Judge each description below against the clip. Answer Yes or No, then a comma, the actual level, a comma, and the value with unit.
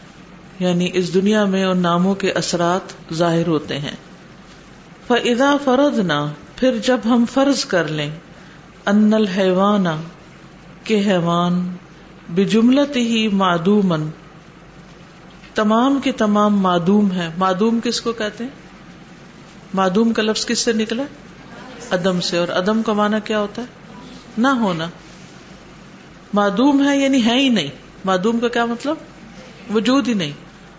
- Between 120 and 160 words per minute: Yes, average, 125 wpm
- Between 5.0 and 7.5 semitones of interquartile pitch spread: No, average, 4.5 semitones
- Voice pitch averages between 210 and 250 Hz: No, high, 195 Hz